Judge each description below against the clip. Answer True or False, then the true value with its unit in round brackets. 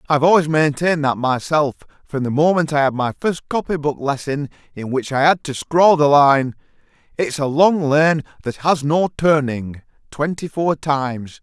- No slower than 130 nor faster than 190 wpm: True (180 wpm)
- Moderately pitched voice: True (145 Hz)